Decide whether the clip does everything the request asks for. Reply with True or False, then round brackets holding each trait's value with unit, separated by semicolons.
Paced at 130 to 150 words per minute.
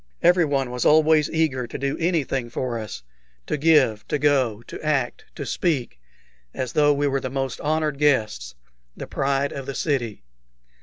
False (170 wpm)